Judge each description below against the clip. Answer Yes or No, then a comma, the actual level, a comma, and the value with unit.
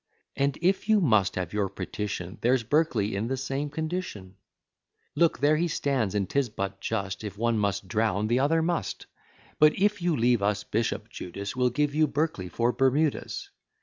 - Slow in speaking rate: No, average, 180 wpm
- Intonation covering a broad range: Yes, wide, 6.9 semitones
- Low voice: Yes, low, 120 Hz